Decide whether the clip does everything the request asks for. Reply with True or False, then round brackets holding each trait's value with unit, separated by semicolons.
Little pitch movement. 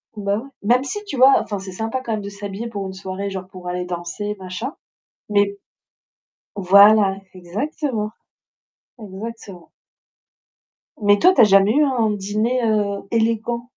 False (3.1 semitones)